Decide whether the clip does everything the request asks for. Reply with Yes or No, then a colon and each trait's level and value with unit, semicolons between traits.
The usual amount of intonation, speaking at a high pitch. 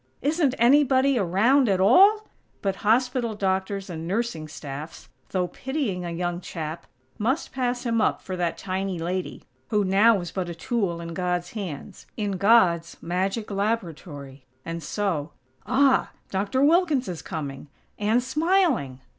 No: wide, 6.1 semitones; high, 195 Hz